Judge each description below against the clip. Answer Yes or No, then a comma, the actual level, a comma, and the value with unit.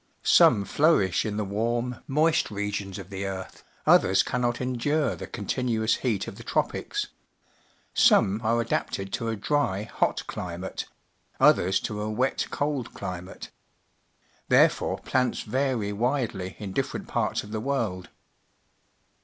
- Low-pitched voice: Yes, low, 110 Hz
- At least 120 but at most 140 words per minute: Yes, slow, 135 wpm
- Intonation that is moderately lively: Yes, average, 4.4 semitones